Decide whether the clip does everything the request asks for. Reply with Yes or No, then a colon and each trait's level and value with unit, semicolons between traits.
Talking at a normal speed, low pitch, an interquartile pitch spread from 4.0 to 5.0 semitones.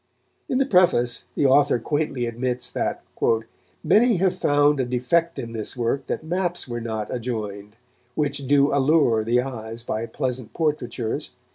Yes: average, 150 wpm; low, 130 Hz; average, 4.4 semitones